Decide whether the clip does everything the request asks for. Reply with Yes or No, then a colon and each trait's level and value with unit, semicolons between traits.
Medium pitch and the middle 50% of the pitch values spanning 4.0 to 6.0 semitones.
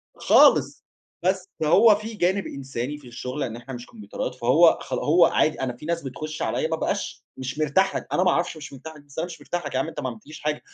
Yes: medium, 150 Hz; average, 4.7 semitones